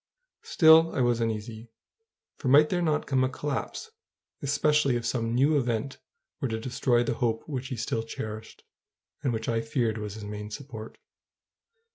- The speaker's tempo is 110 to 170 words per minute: Yes, average, 165 wpm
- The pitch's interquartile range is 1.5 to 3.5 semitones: No, average, 3.9 semitones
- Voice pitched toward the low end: Yes, low, 120 Hz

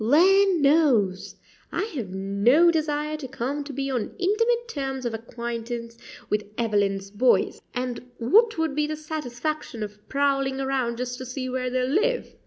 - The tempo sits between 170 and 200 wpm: No, average, 160 wpm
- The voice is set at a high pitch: Yes, very high, 265 Hz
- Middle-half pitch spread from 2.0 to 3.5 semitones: No, average, 4.6 semitones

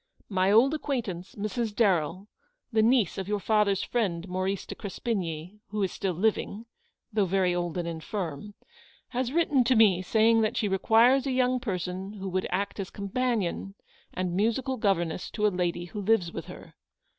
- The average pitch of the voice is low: No, high, 200 Hz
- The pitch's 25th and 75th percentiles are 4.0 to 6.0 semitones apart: No, average, 3.6 semitones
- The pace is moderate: Yes, average, 170 wpm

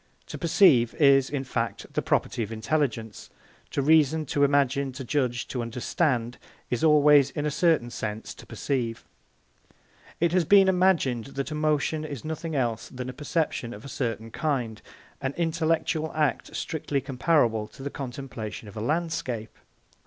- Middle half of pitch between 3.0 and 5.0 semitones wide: Yes, average, 4.6 semitones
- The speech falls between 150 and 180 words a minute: Yes, average, 155 wpm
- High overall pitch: No, medium, 140 Hz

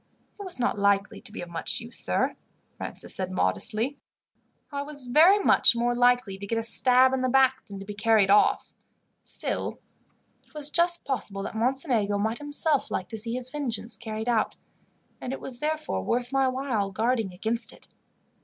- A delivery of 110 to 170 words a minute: No, average, 185 wpm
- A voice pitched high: Yes, high, 240 Hz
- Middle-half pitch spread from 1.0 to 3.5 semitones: No, average, 4.4 semitones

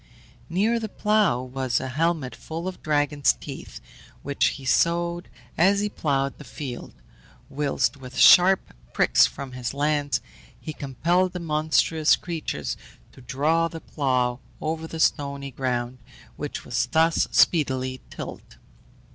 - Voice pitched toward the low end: No, medium, 150 Hz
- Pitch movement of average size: Yes, average, 4.1 semitones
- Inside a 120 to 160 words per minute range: Yes, slow, 135 wpm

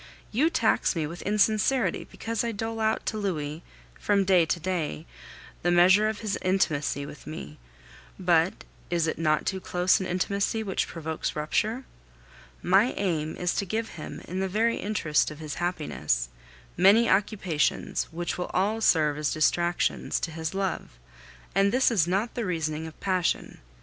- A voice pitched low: No, medium, 180 Hz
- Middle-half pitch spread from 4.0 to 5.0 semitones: Yes, average, 4.5 semitones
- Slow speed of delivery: No, average, 165 wpm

